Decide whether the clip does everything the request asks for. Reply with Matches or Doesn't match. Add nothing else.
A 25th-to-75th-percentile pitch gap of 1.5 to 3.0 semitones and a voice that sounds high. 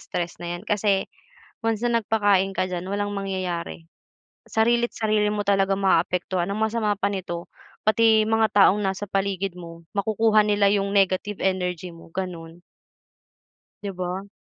Matches